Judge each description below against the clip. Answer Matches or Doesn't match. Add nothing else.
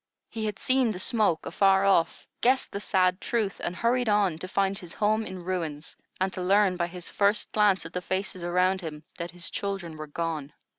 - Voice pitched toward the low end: Doesn't match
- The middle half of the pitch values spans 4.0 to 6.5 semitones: Doesn't match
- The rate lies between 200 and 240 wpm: Matches